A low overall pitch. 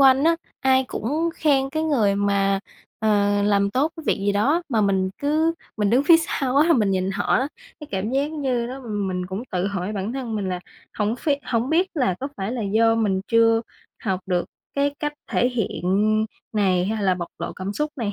No: high, 225 Hz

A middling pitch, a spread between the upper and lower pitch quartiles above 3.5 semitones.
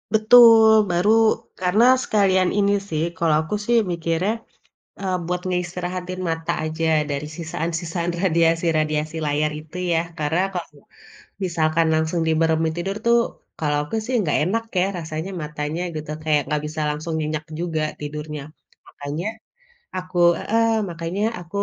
No: medium, 165 Hz; average, 2.8 semitones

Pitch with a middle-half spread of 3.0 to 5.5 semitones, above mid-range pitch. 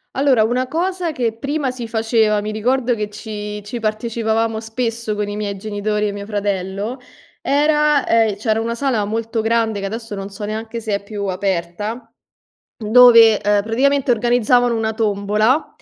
No: narrow, 2.6 semitones; high, 220 Hz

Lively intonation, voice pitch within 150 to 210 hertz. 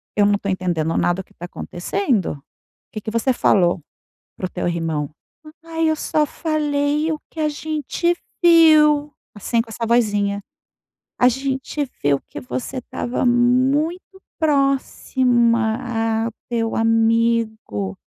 No: wide, 6.3 semitones; high, 240 Hz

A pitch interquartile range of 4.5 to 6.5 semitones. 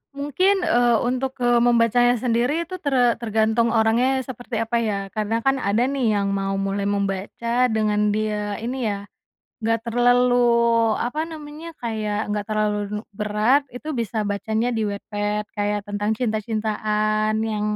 No: average, 2.7 semitones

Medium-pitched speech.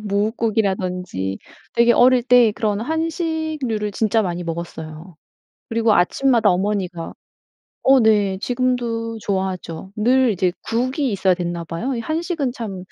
No: high, 220 Hz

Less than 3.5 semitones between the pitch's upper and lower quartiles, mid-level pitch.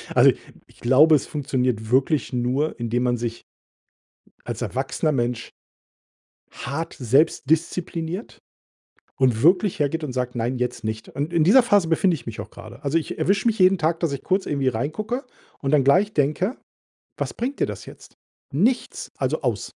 No: wide, 5.5 semitones; medium, 145 Hz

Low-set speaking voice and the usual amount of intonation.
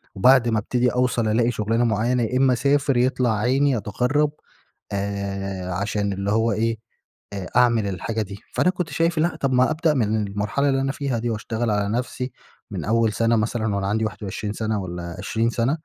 Yes: low, 115 Hz; average, 3.6 semitones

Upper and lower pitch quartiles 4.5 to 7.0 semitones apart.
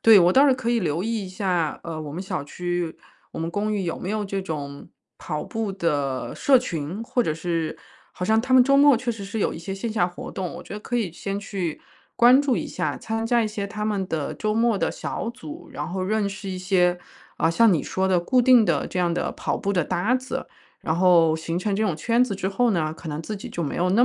Yes: average, 4.8 semitones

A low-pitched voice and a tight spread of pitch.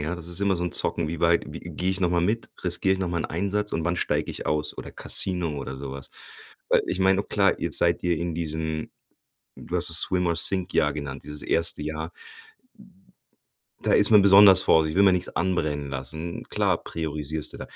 No: very low, 85 Hz; average, 3.2 semitones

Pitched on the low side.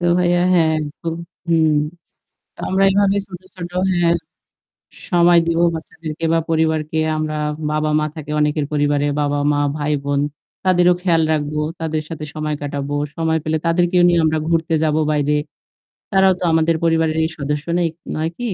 No: medium, 160 Hz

